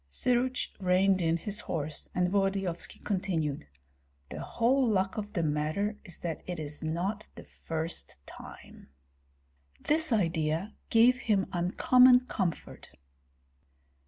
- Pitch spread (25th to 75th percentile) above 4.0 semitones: Yes, average, 4.7 semitones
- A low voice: No, high, 190 Hz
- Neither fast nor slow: No, slow, 120 wpm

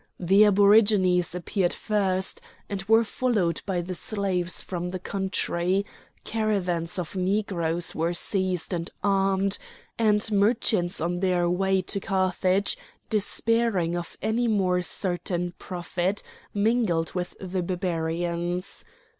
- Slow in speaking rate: Yes, slow, 115 wpm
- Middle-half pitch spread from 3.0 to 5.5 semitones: No, narrow, 2.5 semitones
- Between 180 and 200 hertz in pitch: Yes, medium, 185 Hz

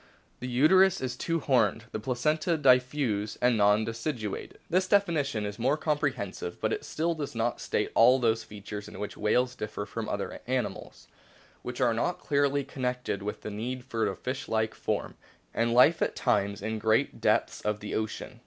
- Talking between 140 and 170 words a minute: No, average, 180 wpm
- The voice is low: Yes, low, 120 Hz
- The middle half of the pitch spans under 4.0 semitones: No, average, 4.9 semitones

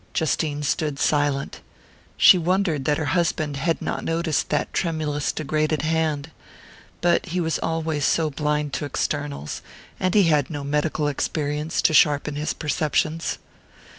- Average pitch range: No, narrow, 1.9 semitones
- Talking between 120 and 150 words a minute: Yes, average, 140 wpm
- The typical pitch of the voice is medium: Yes, medium, 155 Hz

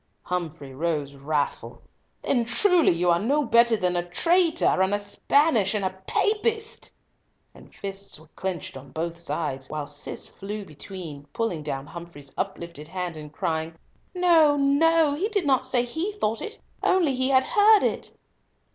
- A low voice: No, high, 195 Hz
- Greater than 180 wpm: No, average, 160 wpm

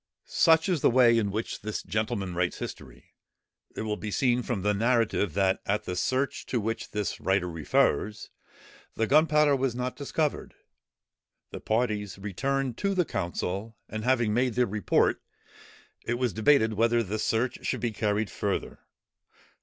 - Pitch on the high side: No, low, 110 Hz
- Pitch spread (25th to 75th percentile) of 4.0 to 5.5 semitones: No, average, 3.6 semitones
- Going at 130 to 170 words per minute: Yes, average, 160 wpm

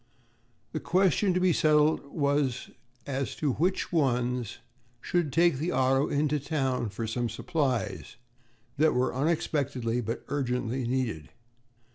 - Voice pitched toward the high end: No, low, 135 Hz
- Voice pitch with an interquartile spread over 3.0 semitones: Yes, average, 3.9 semitones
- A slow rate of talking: Yes, slow, 125 wpm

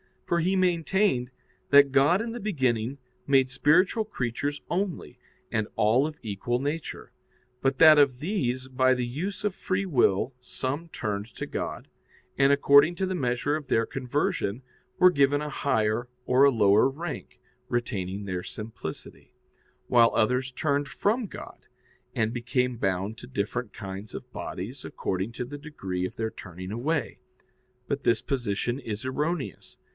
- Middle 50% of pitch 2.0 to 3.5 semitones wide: No, average, 4.9 semitones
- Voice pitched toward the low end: Yes, low, 130 Hz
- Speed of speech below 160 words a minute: Yes, average, 150 wpm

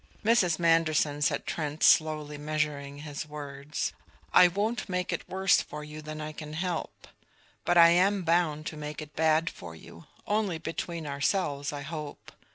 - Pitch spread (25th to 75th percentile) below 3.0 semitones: Yes, narrow, 2.5 semitones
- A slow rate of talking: No, average, 165 wpm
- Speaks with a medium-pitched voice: Yes, medium, 155 Hz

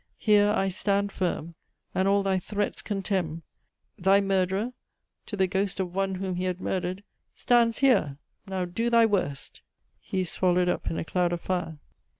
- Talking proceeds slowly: No, average, 170 wpm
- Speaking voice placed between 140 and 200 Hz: Yes, high, 190 Hz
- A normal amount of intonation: No, narrow, 2.0 semitones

